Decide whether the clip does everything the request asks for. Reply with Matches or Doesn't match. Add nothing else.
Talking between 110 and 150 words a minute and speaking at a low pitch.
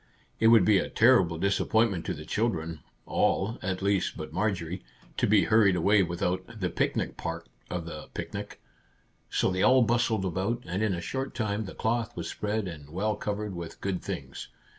Doesn't match